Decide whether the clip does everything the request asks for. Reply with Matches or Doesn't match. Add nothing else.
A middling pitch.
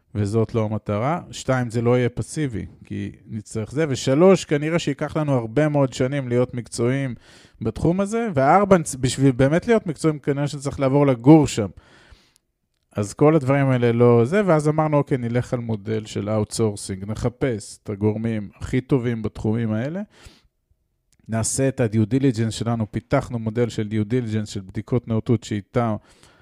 Doesn't match